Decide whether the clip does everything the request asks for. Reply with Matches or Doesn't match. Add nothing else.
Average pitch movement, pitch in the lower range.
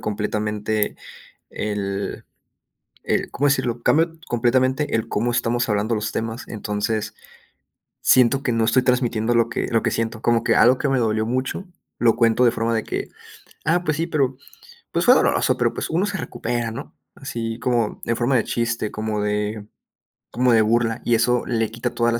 Doesn't match